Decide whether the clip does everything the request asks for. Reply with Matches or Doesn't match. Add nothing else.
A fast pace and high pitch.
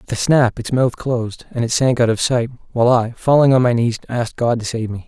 Doesn't match